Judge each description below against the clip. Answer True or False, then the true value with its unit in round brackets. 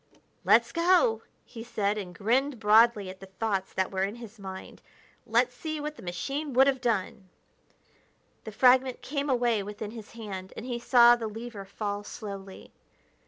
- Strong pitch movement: False (3.8 semitones)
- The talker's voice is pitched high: True (225 Hz)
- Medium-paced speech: True (165 wpm)